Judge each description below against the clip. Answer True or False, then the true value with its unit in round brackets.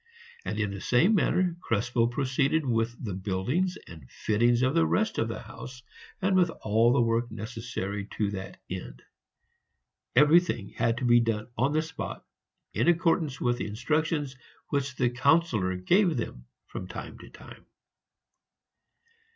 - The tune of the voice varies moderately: False (6.0 semitones)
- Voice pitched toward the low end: True (120 Hz)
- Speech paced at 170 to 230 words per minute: False (150 wpm)